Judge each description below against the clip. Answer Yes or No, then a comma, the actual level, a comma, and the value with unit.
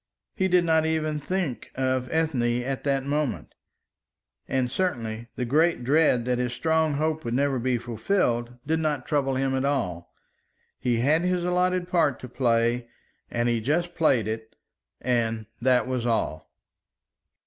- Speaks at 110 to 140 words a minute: No, average, 155 wpm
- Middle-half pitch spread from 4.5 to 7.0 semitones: Yes, average, 4.9 semitones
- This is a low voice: Yes, low, 130 Hz